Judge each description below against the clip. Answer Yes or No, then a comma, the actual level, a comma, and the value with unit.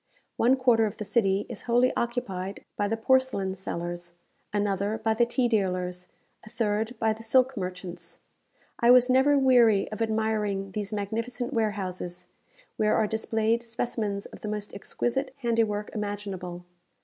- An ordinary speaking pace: Yes, average, 150 wpm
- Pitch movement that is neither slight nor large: Yes, average, 3.2 semitones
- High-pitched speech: Yes, high, 215 Hz